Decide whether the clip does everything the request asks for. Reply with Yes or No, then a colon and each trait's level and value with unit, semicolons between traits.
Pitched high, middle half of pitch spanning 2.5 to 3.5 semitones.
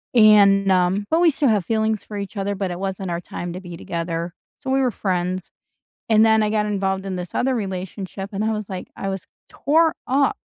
Yes: high, 195 Hz; average, 2.9 semitones